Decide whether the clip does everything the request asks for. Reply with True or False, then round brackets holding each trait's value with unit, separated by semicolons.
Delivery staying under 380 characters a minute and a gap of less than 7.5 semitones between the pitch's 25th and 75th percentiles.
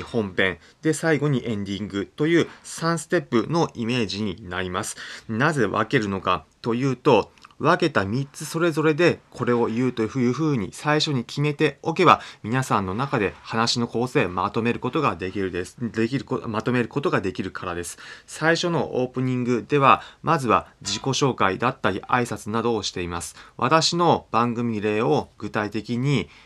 True (310 characters per minute; 5.3 semitones)